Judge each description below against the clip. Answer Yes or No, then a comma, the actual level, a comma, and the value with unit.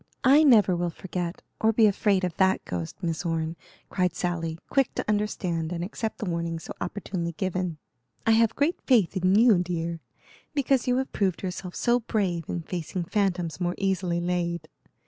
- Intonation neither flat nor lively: Yes, average, 3.8 semitones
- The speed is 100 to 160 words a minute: No, average, 175 wpm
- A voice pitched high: No, medium, 180 Hz